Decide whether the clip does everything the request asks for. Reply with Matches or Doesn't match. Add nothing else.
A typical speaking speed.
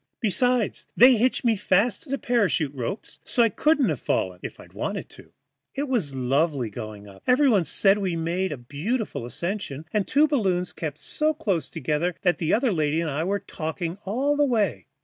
Matches